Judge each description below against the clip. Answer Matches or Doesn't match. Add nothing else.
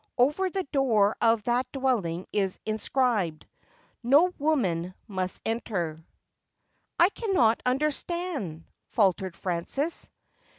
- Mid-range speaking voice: Doesn't match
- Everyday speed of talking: Doesn't match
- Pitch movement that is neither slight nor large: Doesn't match